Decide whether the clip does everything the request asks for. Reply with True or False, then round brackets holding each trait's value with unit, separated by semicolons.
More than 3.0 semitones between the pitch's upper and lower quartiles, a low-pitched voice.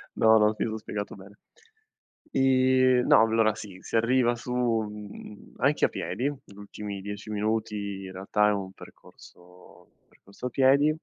True (3.4 semitones; 105 Hz)